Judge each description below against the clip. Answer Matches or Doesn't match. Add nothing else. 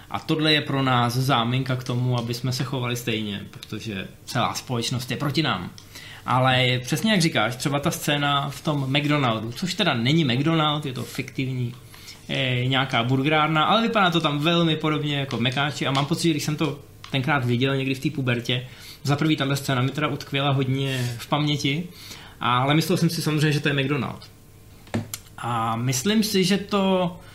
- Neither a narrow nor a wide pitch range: Matches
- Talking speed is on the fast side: Matches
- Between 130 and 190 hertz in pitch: Matches